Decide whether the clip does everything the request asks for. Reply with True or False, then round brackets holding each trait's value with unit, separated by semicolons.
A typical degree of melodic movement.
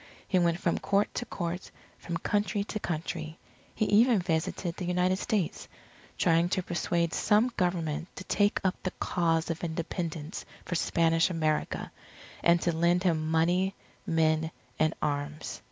False (2.3 semitones)